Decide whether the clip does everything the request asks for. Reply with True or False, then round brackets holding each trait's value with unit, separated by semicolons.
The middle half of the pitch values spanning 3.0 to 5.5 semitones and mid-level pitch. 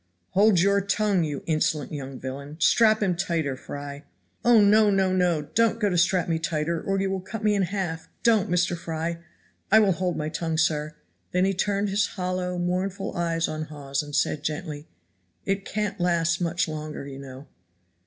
True (4.0 semitones; 175 Hz)